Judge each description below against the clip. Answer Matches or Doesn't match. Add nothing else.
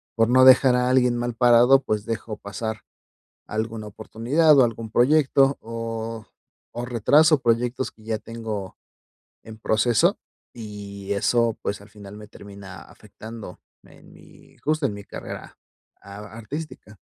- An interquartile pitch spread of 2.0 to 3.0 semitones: Matches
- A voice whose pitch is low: Matches